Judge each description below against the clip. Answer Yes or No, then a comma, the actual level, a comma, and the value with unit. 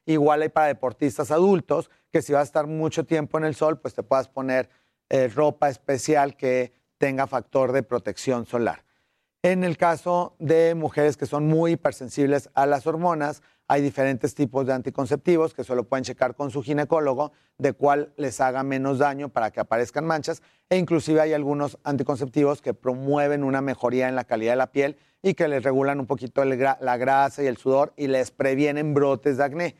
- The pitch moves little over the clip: Yes, narrow, 2.2 semitones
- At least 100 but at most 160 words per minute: No, fast, 190 wpm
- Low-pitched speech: No, medium, 145 Hz